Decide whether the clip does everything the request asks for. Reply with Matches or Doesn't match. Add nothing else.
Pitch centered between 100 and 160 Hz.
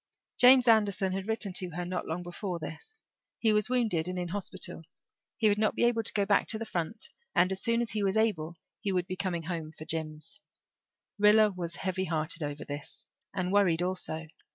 Doesn't match